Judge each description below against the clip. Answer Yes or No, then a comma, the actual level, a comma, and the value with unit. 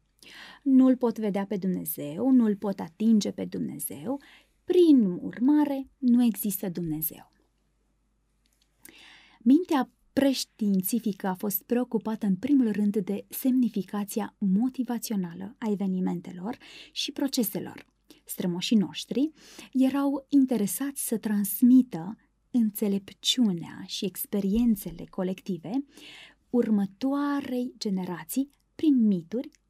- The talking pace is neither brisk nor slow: No, slow, 90 wpm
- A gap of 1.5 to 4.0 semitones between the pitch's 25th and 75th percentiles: No, average, 4.8 semitones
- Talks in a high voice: Yes, high, 225 Hz